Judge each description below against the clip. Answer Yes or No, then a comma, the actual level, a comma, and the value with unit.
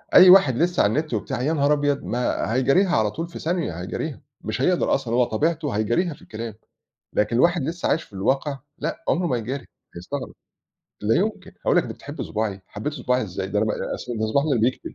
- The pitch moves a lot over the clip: Yes, wide, 6.5 semitones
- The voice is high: No, low, 130 Hz